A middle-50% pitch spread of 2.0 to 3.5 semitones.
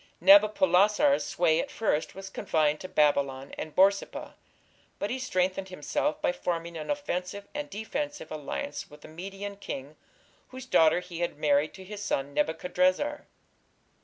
No: average, 4.5 semitones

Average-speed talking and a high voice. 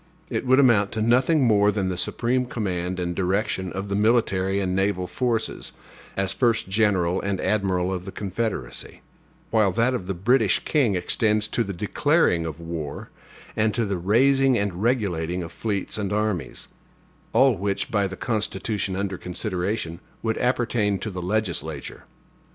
No: average, 160 wpm; low, 100 Hz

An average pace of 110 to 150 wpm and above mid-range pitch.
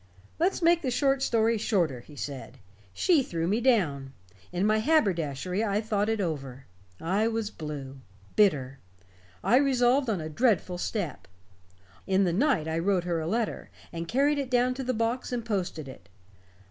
No: average, 170 wpm; high, 205 Hz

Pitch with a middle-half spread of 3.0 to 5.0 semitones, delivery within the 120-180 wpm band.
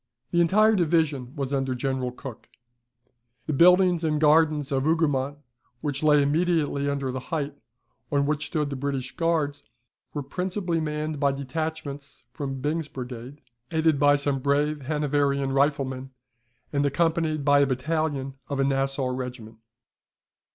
No: narrow, 2.6 semitones; average, 140 wpm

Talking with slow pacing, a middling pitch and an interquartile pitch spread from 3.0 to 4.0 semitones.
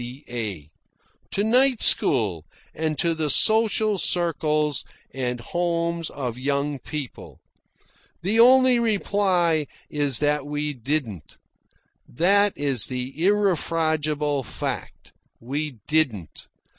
No: slow, 100 wpm; medium, 150 Hz; average, 5.1 semitones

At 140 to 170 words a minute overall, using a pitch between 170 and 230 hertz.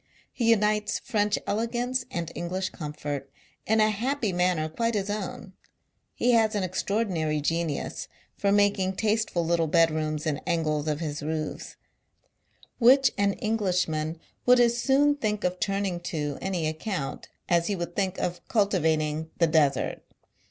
Yes: average, 165 wpm; medium, 185 Hz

